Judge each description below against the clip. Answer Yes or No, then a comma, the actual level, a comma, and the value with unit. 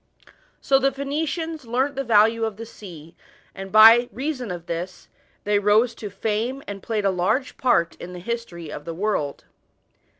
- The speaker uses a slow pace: No, average, 170 wpm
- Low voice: No, high, 220 Hz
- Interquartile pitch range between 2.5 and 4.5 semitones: No, wide, 5.5 semitones